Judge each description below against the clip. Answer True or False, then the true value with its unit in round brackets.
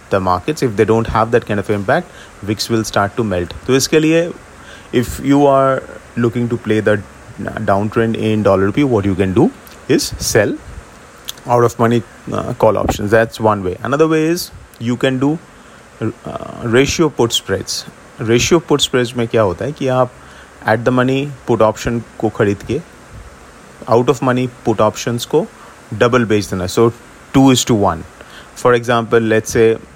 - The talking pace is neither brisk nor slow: True (170 wpm)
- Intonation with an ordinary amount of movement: True (3.2 semitones)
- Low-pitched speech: True (115 Hz)